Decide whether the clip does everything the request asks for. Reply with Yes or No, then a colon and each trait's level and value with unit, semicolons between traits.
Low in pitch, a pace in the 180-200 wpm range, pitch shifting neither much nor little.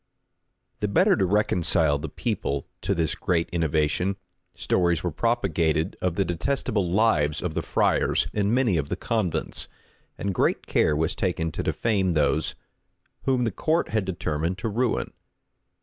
No: very low, 90 Hz; average, 150 wpm; average, 4.5 semitones